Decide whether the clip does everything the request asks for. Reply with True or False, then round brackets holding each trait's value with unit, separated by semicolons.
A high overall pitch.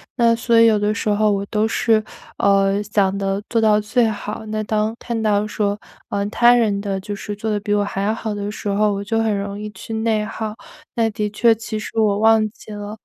True (210 Hz)